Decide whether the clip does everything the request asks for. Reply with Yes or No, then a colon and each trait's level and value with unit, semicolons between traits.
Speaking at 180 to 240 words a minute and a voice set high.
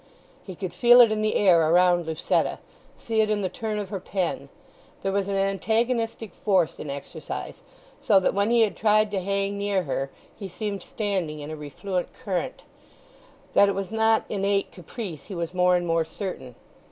Yes: average, 190 wpm; high, 195 Hz